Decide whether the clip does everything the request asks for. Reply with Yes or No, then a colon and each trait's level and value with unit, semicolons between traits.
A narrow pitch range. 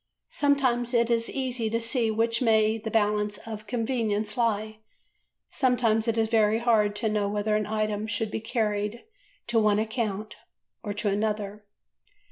Yes: narrow, 1.7 semitones